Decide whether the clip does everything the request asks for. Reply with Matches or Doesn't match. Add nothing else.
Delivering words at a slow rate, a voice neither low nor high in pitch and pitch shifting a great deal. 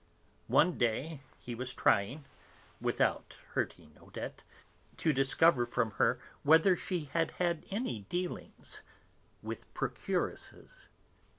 Matches